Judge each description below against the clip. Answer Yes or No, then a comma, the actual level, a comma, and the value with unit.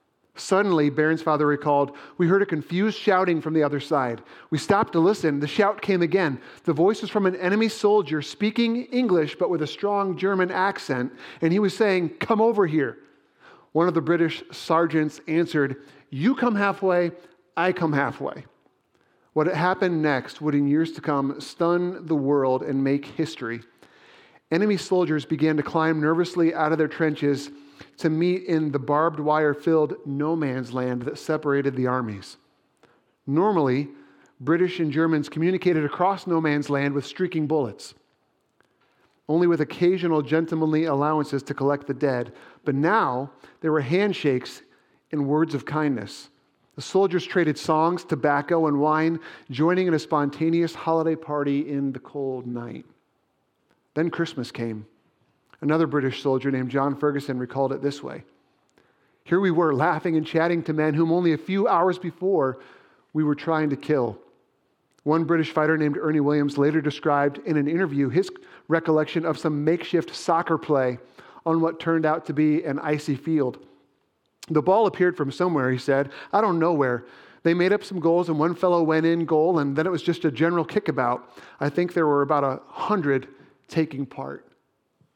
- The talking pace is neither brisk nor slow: Yes, average, 170 wpm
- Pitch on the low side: No, medium, 155 Hz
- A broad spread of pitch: No, average, 3.3 semitones